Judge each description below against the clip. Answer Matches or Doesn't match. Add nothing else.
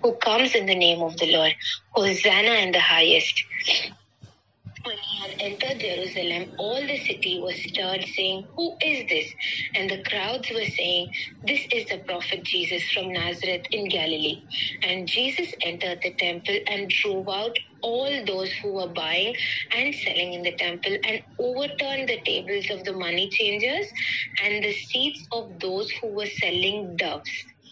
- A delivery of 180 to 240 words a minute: Doesn't match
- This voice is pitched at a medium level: Doesn't match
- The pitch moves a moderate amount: Matches